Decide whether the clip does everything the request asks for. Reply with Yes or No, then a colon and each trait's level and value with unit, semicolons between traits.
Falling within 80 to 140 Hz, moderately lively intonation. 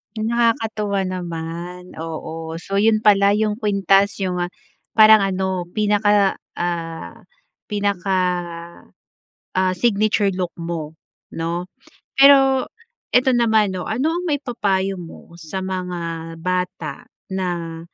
No: high, 190 Hz; average, 3.5 semitones